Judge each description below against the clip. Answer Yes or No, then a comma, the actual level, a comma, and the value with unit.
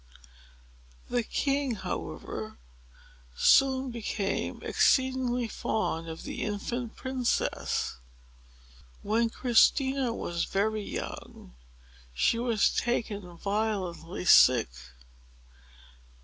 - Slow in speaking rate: Yes, slow, 80 wpm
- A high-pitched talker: Yes, high, 225 Hz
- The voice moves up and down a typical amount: Yes, average, 4.2 semitones